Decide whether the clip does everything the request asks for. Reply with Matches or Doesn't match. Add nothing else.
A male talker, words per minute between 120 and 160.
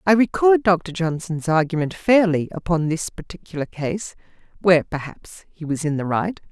Doesn't match